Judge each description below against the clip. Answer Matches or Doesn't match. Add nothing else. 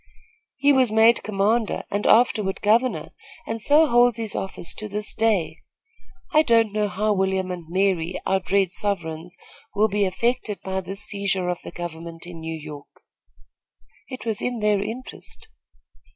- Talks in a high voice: Matches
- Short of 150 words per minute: Doesn't match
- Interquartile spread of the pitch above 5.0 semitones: Doesn't match